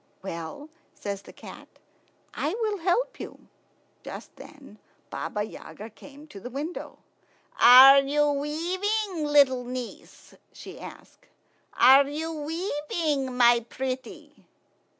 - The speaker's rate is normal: No, slow, 110 wpm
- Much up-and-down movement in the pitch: No, average, 4.2 semitones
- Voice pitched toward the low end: No, very high, 285 Hz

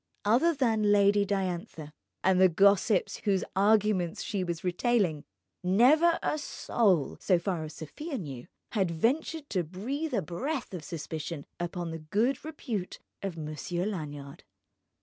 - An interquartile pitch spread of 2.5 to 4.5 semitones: No, average, 5.3 semitones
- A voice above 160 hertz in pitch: Yes, high, 190 Hz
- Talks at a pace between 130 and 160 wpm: Yes, average, 140 wpm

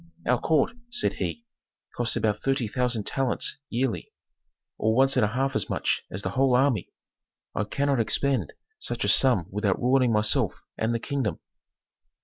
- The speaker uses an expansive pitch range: No, average, 3.9 semitones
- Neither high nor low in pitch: No, low, 125 Hz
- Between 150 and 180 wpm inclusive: Yes, average, 160 wpm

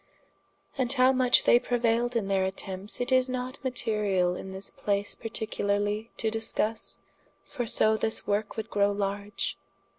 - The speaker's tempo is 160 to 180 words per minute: No, average, 150 wpm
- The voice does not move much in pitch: No, average, 3.2 semitones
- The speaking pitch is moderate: No, high, 220 Hz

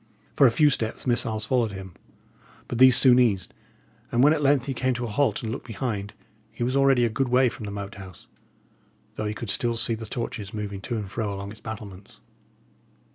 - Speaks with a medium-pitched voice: No, low, 115 Hz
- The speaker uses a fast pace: Yes, fast, 215 wpm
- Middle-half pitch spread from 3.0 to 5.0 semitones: Yes, average, 3.6 semitones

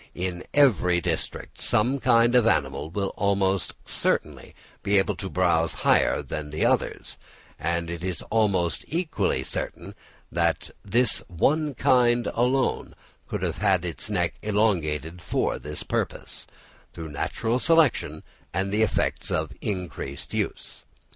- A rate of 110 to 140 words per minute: Yes, slow, 135 wpm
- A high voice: No, very low, 95 Hz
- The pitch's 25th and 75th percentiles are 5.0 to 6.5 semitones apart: Yes, wide, 5.5 semitones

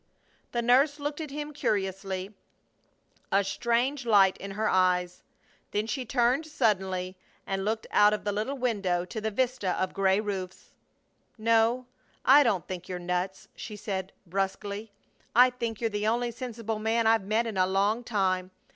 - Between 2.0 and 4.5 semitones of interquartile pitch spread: Yes, average, 3.7 semitones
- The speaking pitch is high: Yes, high, 210 Hz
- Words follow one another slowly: No, average, 165 wpm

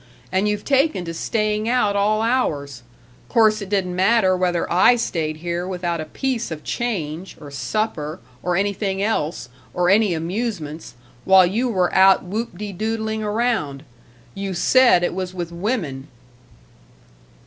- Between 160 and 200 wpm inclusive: No, average, 150 wpm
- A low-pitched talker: No, high, 190 Hz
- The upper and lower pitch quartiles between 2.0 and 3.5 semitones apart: No, average, 4.1 semitones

